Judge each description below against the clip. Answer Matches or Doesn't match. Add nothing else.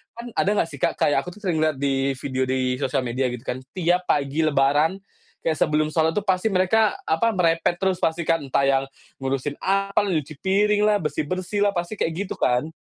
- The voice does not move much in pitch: Doesn't match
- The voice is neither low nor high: Matches